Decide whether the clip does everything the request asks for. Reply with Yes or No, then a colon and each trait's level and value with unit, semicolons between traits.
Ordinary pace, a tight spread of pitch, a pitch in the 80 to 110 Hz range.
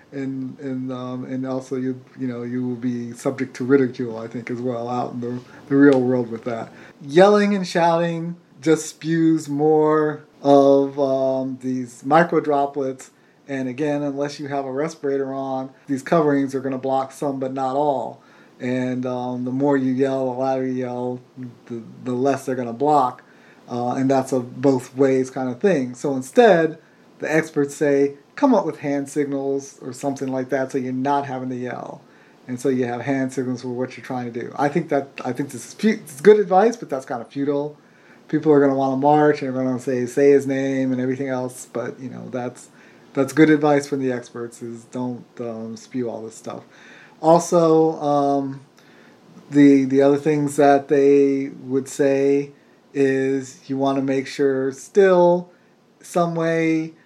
No: average, 190 wpm; narrow, 2.2 semitones; low, 135 Hz